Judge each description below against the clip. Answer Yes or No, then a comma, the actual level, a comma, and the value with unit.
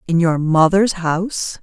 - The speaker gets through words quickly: No, average, 150 wpm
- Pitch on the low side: No, medium, 175 Hz